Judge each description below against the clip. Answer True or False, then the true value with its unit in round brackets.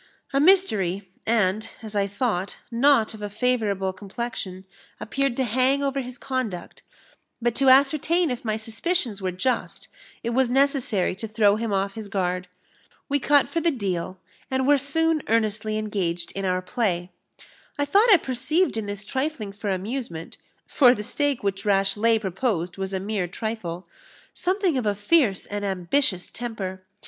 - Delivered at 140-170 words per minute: True (160 wpm)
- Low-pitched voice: False (220 Hz)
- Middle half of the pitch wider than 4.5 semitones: True (5.3 semitones)